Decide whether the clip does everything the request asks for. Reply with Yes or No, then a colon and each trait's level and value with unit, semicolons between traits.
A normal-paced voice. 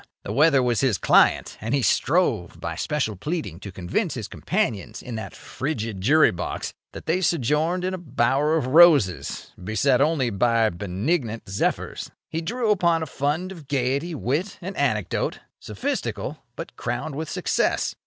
Yes: average, 160 wpm